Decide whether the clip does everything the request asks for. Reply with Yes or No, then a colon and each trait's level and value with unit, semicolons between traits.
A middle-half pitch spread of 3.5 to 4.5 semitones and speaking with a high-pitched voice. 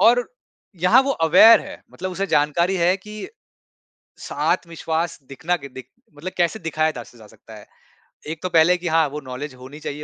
No: average, 4.0 semitones; medium, 165 Hz